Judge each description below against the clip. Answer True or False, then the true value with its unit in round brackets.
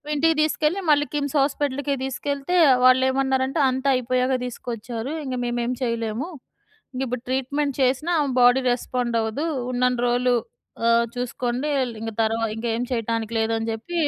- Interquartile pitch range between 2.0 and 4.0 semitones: True (2.9 semitones)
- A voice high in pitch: True (255 Hz)